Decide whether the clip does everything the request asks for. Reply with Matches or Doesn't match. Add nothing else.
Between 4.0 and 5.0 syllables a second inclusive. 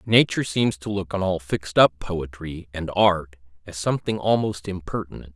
Doesn't match